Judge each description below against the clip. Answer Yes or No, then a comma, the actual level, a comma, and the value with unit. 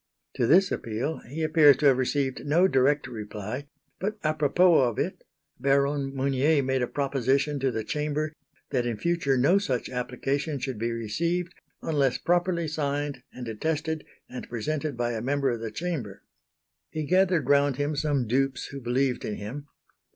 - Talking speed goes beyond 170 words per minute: No, average, 165 wpm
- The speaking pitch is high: No, medium, 140 Hz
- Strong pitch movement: No, average, 3.6 semitones